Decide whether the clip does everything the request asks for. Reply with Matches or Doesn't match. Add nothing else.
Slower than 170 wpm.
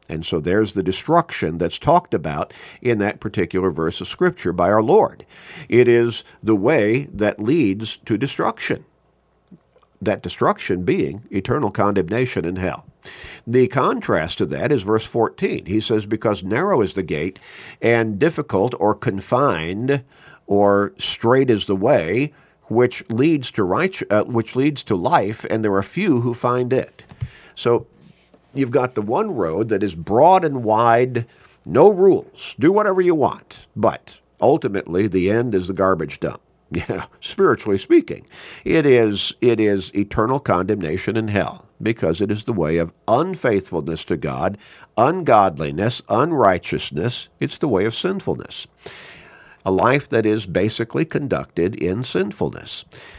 Matches